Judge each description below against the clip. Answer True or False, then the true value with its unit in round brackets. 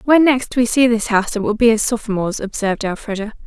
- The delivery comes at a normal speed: False (225 wpm)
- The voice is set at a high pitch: True (225 Hz)